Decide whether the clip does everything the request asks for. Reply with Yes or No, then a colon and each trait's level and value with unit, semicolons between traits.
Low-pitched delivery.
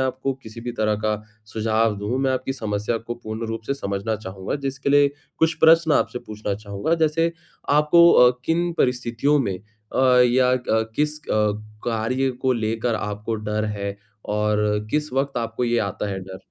Yes: low, 120 Hz